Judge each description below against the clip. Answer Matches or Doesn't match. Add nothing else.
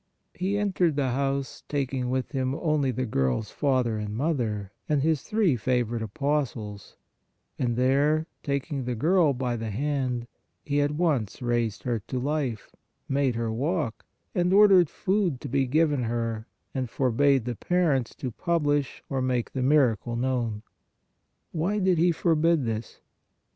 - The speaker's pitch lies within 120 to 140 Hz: Matches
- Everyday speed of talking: Matches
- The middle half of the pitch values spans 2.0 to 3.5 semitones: Doesn't match